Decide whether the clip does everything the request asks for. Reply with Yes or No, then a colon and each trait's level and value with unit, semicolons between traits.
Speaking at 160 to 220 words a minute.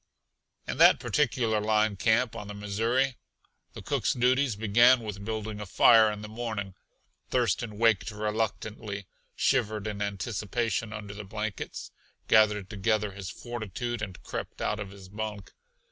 No: average, 145 wpm